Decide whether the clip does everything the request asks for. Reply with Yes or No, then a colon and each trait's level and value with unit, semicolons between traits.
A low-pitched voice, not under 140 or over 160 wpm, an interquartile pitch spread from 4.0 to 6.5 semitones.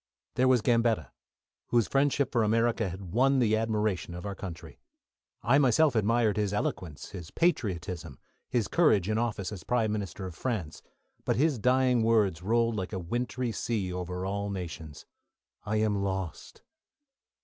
Yes: low, 105 Hz; average, 155 wpm; average, 4.3 semitones